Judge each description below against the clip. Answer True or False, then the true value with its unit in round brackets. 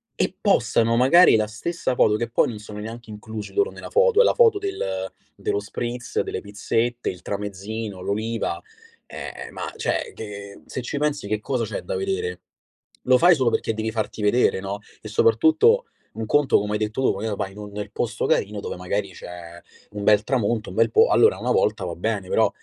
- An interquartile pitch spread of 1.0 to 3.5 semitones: False (5.1 semitones)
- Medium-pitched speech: False (110 Hz)